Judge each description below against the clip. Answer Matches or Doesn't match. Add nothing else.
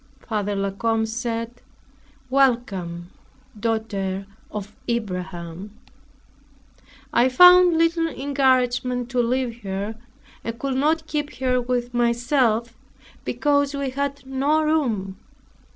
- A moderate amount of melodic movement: Matches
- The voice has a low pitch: Doesn't match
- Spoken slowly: Matches